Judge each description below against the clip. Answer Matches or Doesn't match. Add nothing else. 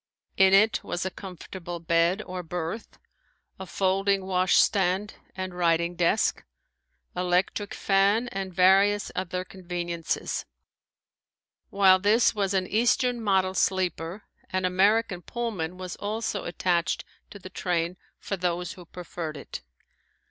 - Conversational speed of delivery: Doesn't match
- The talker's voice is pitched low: Doesn't match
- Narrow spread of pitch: Matches